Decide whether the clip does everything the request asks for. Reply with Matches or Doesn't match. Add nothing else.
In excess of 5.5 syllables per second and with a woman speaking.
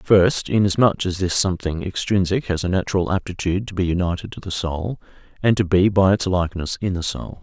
Doesn't match